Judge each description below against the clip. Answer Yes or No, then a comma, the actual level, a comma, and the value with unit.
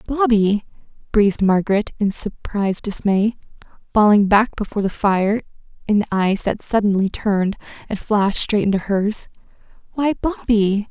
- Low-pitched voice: No, high, 210 Hz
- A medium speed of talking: No, slow, 130 wpm